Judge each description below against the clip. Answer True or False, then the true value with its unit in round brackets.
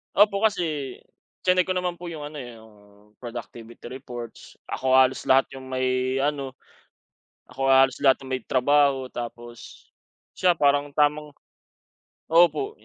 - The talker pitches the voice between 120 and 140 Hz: True (135 Hz)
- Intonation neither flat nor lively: True (3.0 semitones)